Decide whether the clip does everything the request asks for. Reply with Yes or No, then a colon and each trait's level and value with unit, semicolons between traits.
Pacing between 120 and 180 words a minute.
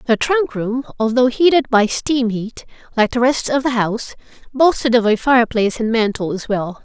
No: average, 195 wpm